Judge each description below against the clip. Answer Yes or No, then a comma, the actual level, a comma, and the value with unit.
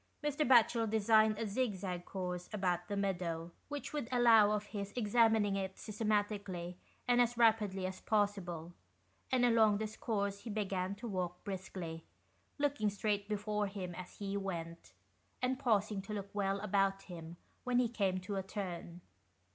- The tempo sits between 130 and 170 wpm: Yes, average, 160 wpm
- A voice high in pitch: Yes, high, 205 Hz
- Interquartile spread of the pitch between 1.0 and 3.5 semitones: Yes, average, 2.9 semitones